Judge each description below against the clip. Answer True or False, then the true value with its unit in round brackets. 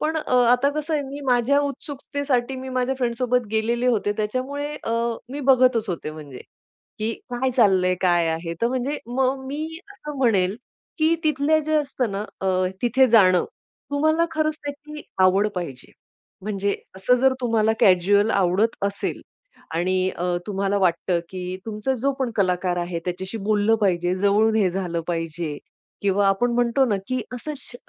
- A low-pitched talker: False (225 Hz)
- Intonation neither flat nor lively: False (5.9 semitones)